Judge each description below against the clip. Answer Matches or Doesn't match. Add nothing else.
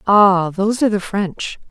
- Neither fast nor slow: Matches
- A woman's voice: Matches